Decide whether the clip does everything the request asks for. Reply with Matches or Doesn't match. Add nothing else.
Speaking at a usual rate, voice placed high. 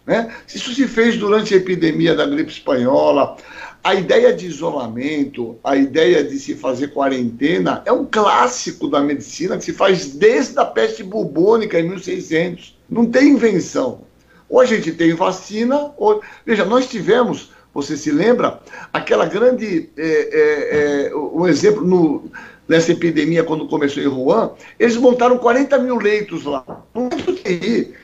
Matches